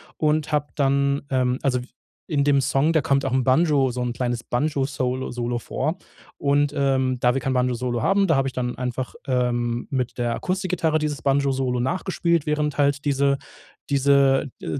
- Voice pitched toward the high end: No, low, 135 Hz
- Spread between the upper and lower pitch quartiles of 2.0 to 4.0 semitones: Yes, narrow, 2.5 semitones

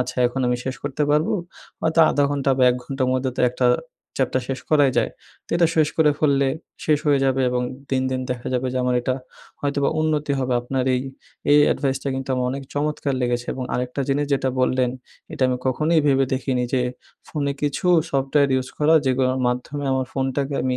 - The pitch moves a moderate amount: No, narrow, 1.9 semitones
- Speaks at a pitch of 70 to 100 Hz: No, low, 135 Hz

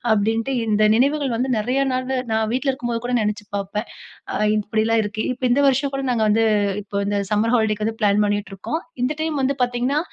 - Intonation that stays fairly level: No, average, 3.6 semitones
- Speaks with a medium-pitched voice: No, high, 225 Hz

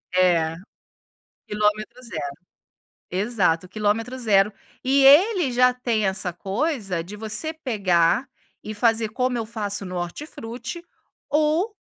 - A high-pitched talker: Yes, high, 220 Hz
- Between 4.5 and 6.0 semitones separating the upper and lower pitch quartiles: Yes, average, 4.8 semitones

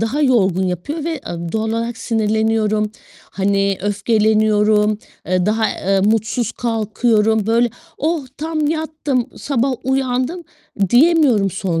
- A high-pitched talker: Yes, high, 220 Hz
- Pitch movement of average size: Yes, average, 3.8 semitones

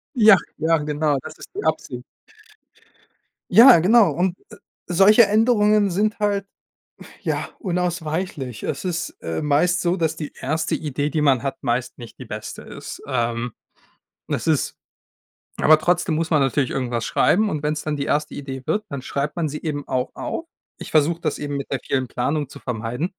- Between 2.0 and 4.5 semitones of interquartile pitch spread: No, average, 4.9 semitones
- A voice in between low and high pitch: Yes, medium, 155 Hz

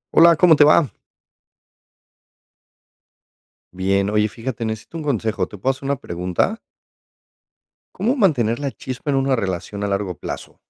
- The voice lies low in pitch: Yes, low, 125 Hz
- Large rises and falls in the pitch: Yes, wide, 6.1 semitones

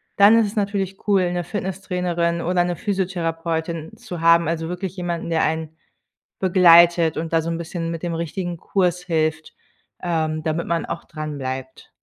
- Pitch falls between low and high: Yes, medium, 170 Hz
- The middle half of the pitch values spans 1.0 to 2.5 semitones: Yes, narrow, 1.9 semitones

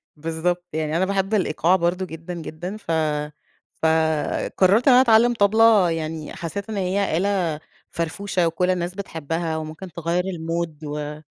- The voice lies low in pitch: No, medium, 175 Hz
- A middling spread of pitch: Yes, average, 3.3 semitones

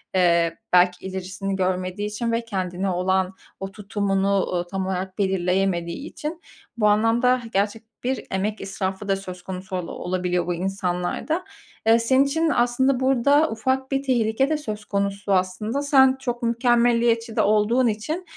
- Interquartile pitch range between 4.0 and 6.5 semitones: Yes, average, 4.4 semitones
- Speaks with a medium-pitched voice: No, high, 205 Hz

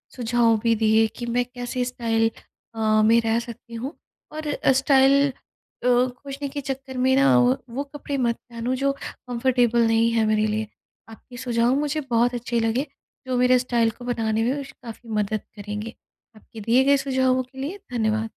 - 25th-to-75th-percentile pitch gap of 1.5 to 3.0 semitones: Yes, narrow, 2.5 semitones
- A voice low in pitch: No, high, 245 Hz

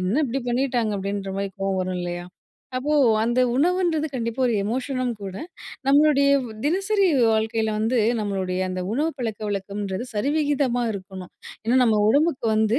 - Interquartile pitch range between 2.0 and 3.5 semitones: No, wide, 5.6 semitones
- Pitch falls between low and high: No, high, 230 Hz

